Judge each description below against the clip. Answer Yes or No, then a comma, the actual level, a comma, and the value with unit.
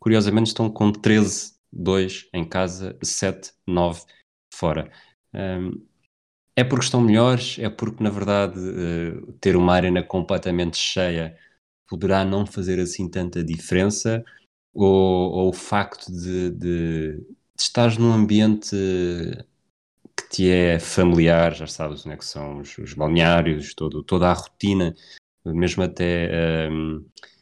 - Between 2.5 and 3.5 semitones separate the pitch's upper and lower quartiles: Yes, average, 3.1 semitones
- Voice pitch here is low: Yes, very low, 90 Hz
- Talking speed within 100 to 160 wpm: Yes, average, 125 wpm